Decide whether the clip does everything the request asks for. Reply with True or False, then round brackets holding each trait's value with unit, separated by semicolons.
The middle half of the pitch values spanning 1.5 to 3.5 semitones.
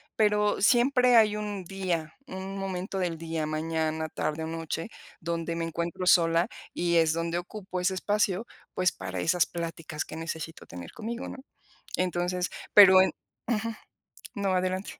True (3.0 semitones)